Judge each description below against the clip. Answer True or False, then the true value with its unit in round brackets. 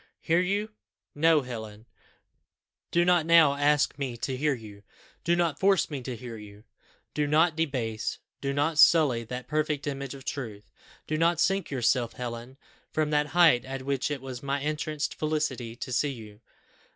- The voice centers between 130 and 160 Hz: True (140 Hz)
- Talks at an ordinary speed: True (170 wpm)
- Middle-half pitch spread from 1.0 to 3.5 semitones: False (3.9 semitones)